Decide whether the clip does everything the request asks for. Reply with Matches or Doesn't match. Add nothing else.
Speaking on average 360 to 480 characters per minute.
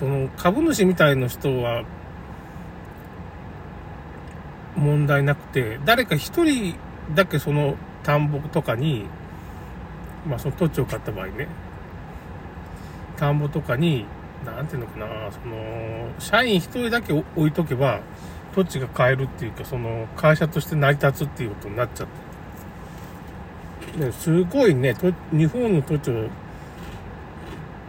Doesn't match